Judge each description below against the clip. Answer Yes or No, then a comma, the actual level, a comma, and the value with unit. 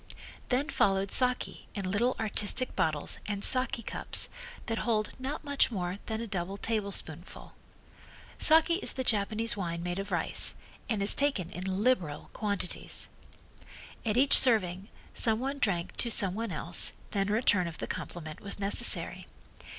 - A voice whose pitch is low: No, high, 205 Hz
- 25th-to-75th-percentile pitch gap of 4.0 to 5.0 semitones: Yes, average, 4.6 semitones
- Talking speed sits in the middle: Yes, average, 155 wpm